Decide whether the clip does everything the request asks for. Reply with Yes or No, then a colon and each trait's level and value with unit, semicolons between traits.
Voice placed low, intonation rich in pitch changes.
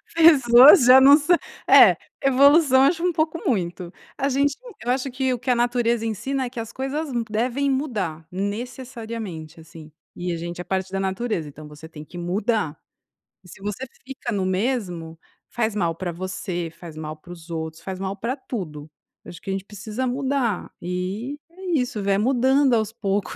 No: high, 220 Hz; wide, 6.7 semitones